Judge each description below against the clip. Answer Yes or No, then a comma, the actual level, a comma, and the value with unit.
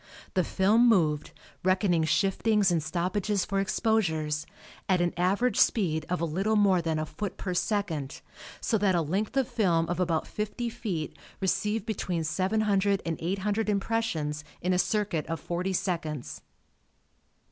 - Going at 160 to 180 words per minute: No, average, 150 wpm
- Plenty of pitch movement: No, average, 4.0 semitones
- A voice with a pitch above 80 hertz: Yes, medium, 185 Hz